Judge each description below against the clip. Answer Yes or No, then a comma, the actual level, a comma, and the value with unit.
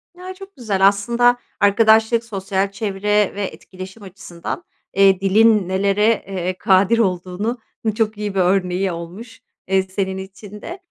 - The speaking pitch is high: Yes, high, 200 Hz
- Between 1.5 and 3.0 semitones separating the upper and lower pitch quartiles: Yes, average, 2.7 semitones